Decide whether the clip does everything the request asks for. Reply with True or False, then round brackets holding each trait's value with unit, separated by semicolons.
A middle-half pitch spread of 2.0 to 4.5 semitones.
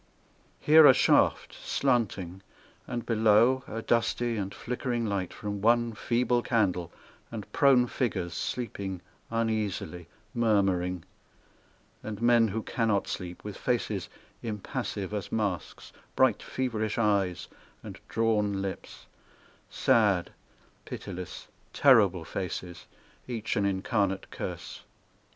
True (3.5 semitones)